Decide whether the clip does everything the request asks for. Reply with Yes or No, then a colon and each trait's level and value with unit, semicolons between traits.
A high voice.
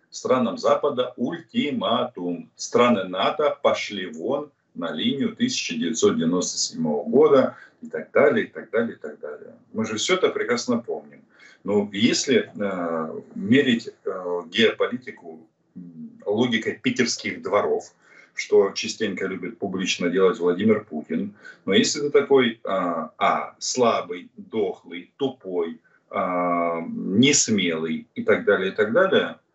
Yes: high, 220 Hz